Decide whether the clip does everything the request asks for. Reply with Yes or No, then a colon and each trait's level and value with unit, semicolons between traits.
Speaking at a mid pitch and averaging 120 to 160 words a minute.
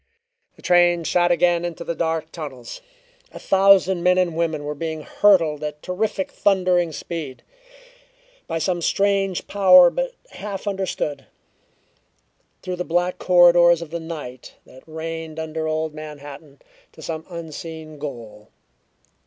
Yes: medium, 170 Hz; slow, 135 wpm